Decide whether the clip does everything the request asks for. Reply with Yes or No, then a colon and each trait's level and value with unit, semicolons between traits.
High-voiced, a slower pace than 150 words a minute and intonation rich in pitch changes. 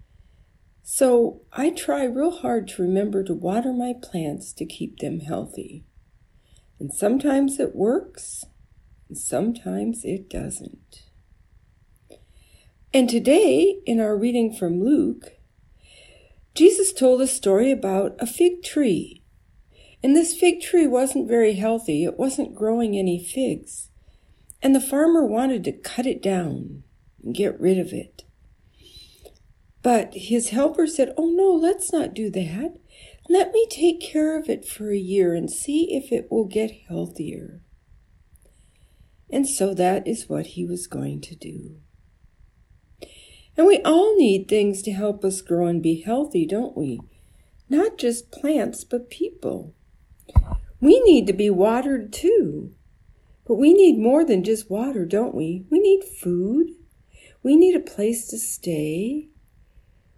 Yes: high, 235 Hz; average, 140 wpm; wide, 8.2 semitones